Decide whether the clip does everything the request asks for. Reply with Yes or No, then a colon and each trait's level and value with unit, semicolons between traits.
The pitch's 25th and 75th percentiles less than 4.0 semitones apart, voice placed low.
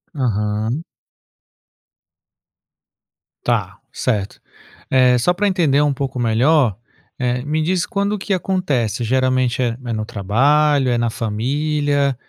No: average, 4.3 semitones; low, 130 Hz